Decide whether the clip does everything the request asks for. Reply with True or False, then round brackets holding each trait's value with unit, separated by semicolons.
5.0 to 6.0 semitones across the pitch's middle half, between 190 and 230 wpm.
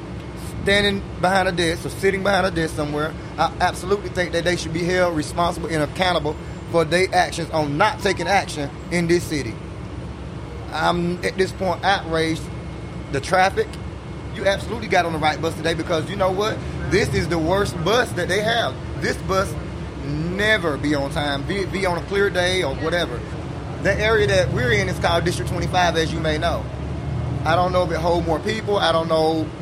False (2.5 semitones; 195 wpm)